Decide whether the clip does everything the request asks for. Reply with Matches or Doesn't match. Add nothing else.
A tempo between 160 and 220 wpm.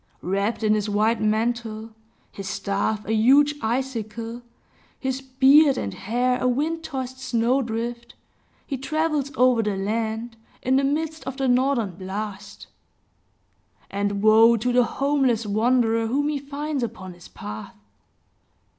Doesn't match